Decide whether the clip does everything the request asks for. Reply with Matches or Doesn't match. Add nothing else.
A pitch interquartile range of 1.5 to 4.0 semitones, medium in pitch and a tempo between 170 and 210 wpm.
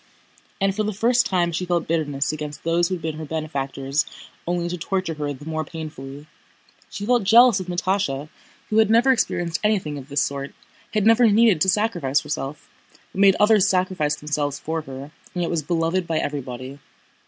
Doesn't match